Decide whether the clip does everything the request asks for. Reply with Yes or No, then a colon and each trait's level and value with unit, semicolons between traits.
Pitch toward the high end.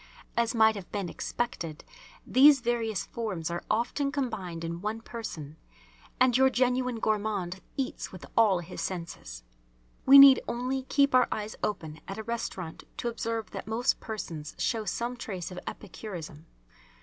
Yes: high, 220 Hz